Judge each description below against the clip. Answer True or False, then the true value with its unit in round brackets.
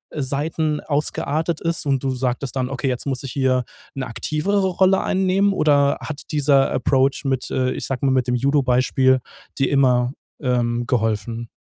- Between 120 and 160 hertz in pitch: True (135 Hz)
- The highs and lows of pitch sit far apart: False (2.9 semitones)